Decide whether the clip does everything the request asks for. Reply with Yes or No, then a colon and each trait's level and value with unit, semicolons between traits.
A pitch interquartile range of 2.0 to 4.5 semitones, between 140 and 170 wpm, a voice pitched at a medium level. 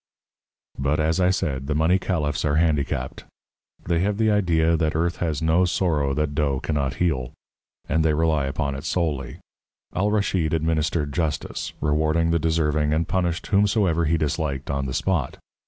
No: average, 2.7 semitones; average, 165 wpm; very low, 80 Hz